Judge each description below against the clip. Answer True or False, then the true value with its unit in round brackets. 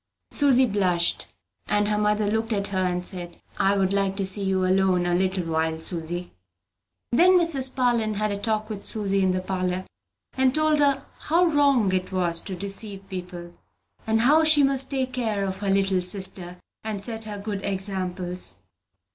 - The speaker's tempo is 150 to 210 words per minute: True (180 wpm)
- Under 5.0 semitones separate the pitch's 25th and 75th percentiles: True (3.4 semitones)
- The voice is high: True (200 Hz)